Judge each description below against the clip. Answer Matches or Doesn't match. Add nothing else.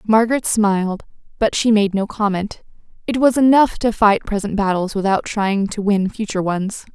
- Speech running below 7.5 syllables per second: Matches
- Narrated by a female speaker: Matches